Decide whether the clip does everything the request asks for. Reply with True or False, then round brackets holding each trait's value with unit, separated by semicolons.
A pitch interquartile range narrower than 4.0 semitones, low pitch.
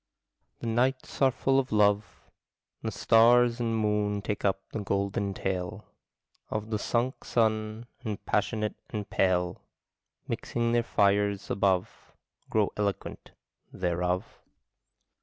True (2.7 semitones; 105 Hz)